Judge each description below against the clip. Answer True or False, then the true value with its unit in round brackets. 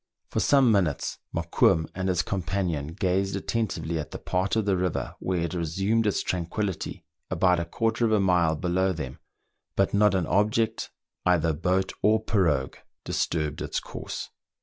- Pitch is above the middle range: False (95 Hz)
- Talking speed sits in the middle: True (160 wpm)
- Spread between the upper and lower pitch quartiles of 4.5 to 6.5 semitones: False (3.3 semitones)